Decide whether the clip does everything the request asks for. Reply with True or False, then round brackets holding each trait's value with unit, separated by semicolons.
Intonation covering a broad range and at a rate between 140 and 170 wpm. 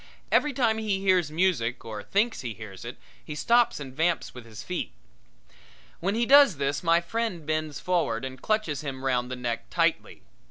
False (7.6 semitones; 185 wpm)